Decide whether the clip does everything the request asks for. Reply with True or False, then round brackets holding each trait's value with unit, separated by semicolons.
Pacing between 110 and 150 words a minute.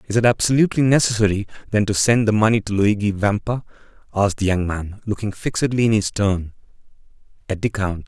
False (180 wpm)